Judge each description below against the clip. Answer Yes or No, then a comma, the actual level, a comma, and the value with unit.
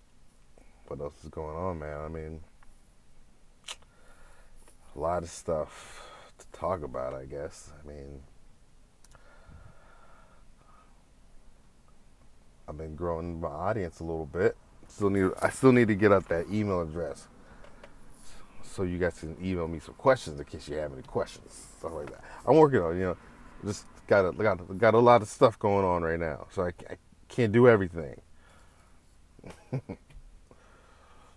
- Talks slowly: No, average, 155 wpm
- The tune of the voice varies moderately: Yes, average, 3.8 semitones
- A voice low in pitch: Yes, very low, 85 Hz